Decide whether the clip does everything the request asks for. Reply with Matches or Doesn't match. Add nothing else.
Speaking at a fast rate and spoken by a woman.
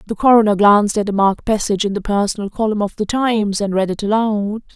Matches